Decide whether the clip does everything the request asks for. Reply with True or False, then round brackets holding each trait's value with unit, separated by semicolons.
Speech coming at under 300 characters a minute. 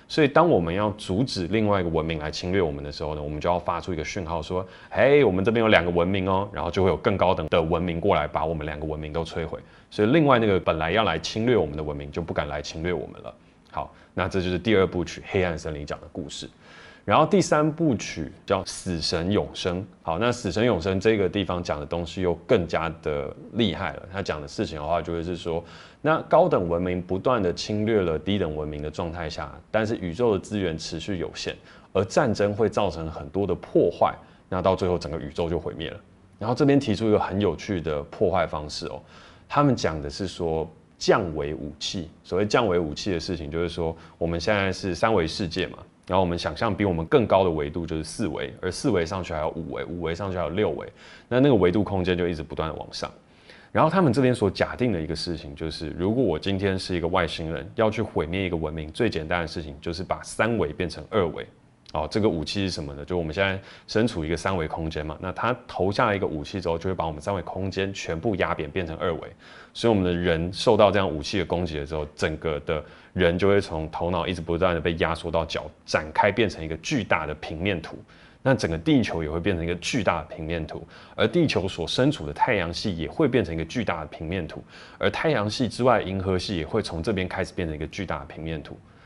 False (350 characters per minute)